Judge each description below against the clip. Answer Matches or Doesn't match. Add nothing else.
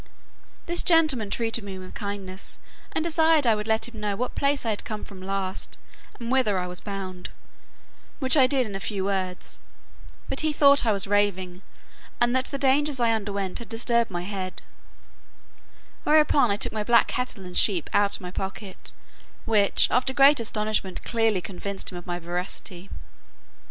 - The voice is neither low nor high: Doesn't match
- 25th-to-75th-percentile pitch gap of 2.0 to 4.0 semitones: Doesn't match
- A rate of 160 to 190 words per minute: Matches